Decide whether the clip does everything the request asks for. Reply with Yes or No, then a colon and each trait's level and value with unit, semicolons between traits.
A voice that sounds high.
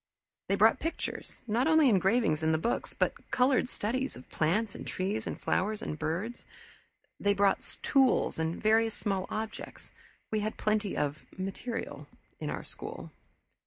Yes: high, 215 Hz